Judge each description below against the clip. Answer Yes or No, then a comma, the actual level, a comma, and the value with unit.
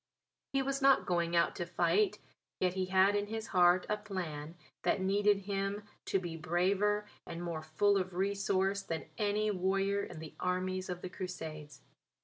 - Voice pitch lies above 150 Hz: Yes, high, 190 Hz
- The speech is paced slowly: No, average, 170 wpm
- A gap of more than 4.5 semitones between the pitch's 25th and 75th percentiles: No, narrow, 2.6 semitones